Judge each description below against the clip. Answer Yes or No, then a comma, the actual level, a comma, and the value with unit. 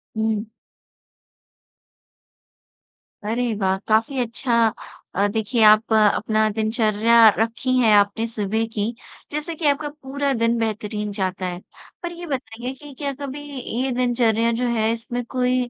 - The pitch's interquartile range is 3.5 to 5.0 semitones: No, average, 3.0 semitones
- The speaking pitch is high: Yes, high, 230 Hz